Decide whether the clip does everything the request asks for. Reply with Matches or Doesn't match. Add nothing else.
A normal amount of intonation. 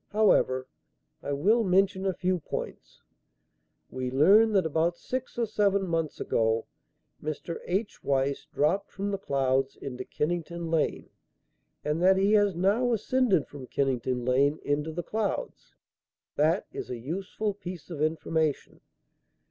Doesn't match